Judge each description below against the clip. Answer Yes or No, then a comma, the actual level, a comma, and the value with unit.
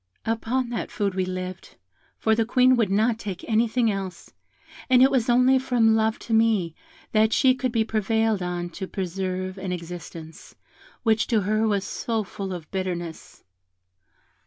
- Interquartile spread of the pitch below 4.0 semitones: Yes, average, 3.5 semitones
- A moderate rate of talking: Yes, average, 160 wpm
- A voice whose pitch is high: Yes, high, 215 Hz